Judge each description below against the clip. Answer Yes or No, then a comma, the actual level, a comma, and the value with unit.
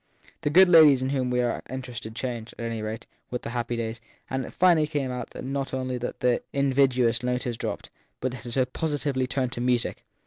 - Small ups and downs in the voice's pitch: Yes, narrow, 2.2 semitones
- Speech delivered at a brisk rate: Yes, fast, 215 wpm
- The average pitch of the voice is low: Yes, low, 125 Hz